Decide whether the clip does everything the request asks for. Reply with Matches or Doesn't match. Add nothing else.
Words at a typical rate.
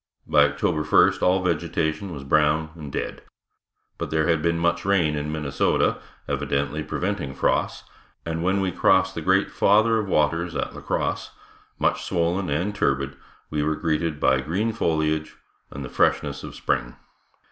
Matches